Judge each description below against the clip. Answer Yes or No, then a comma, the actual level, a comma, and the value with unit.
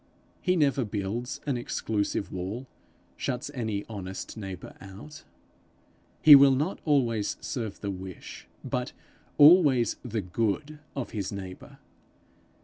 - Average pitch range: No, wide, 5.7 semitones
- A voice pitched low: Yes, low, 115 Hz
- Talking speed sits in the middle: No, slow, 120 wpm